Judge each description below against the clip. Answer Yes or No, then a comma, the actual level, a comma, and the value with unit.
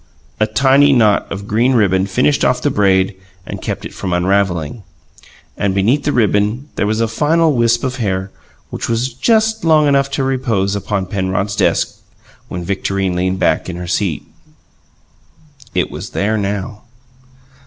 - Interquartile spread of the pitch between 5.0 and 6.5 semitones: Yes, wide, 5.4 semitones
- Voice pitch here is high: No, low, 105 Hz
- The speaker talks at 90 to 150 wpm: No, average, 160 wpm